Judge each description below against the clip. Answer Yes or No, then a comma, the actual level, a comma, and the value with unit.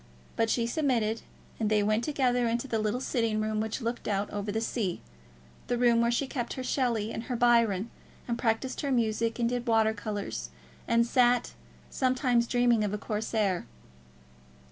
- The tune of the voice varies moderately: No, narrow, 2.2 semitones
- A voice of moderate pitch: No, high, 230 Hz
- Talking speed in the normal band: Yes, average, 175 wpm